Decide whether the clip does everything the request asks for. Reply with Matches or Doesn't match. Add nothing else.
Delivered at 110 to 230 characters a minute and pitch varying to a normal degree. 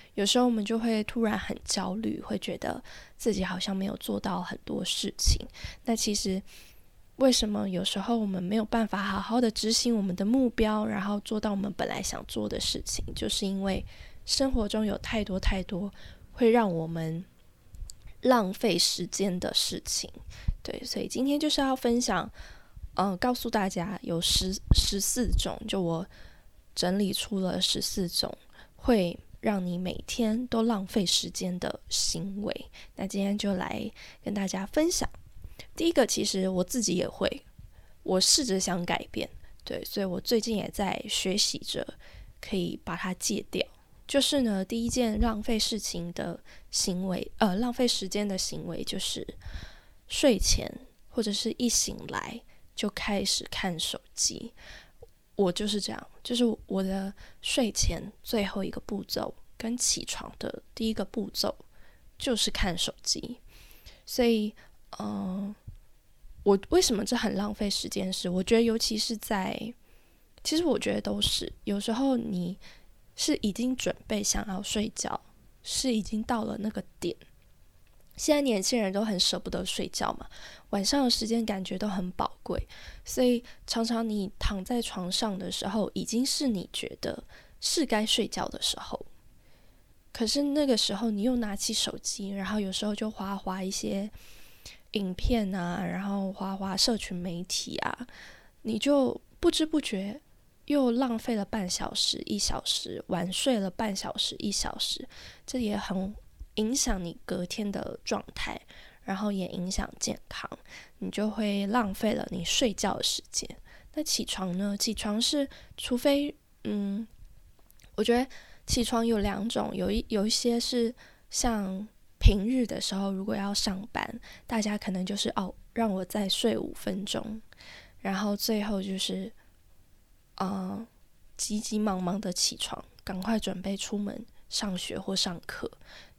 Matches